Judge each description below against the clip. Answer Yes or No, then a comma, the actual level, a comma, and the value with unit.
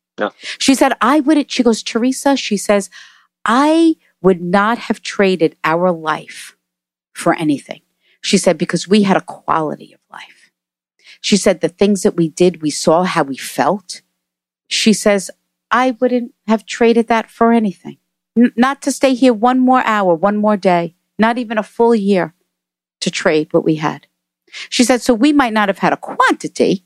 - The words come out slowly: No, average, 175 wpm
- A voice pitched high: Yes, high, 205 Hz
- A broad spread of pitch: Yes, wide, 6.3 semitones